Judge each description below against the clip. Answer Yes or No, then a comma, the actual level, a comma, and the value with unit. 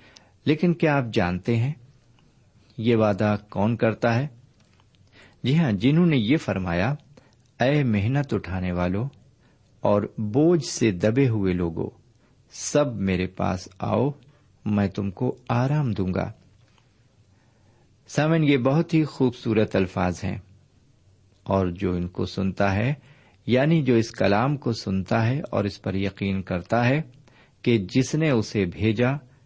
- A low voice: Yes, low, 115 Hz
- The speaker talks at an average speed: Yes, average, 135 wpm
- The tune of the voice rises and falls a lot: No, average, 4.9 semitones